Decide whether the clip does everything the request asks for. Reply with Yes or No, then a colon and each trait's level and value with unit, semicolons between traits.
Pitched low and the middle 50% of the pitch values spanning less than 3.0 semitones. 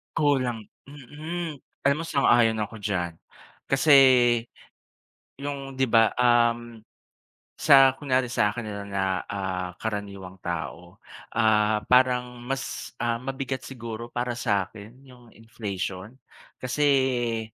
No: low, 120 Hz; average, 3.8 semitones